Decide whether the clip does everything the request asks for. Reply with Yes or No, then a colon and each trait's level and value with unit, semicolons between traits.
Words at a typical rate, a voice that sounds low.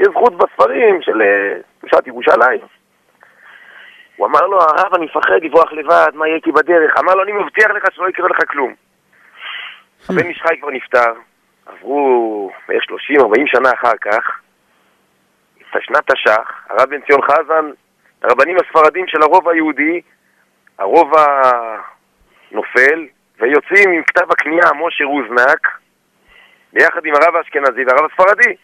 No: average, 130 wpm; medium, 185 Hz